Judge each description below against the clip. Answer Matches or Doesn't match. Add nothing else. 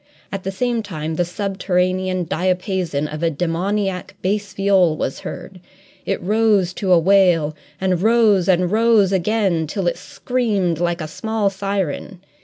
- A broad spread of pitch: Doesn't match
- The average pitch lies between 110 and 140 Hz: Doesn't match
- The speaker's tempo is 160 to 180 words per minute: Doesn't match